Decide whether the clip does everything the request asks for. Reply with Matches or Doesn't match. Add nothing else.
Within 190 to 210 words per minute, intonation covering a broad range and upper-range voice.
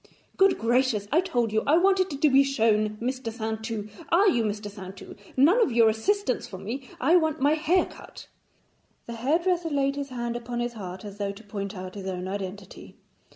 Matches